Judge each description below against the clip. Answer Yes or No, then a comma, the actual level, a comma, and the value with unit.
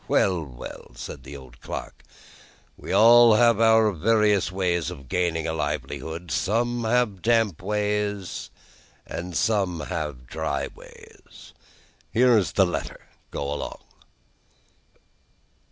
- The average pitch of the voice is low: Yes, very low, 95 Hz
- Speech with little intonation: No, wide, 5.6 semitones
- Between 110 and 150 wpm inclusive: Yes, slow, 135 wpm